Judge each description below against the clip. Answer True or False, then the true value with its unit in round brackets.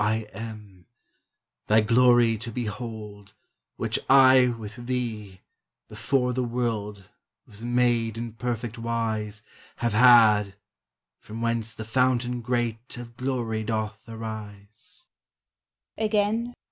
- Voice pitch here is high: False (115 Hz)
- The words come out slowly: True (105 wpm)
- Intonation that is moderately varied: False (2.2 semitones)